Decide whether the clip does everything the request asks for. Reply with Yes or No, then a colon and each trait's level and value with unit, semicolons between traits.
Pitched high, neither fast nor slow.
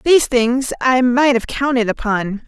Yes: very high, 250 Hz; average, 170 wpm